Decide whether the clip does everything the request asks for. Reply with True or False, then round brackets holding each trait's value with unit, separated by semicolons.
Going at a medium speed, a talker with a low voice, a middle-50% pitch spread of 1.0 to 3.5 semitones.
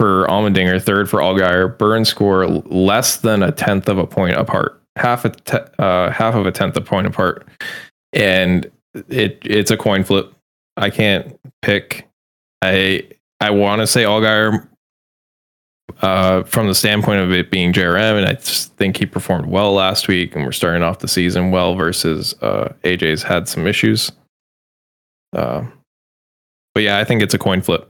True (175 wpm; 95 Hz; 2.4 semitones)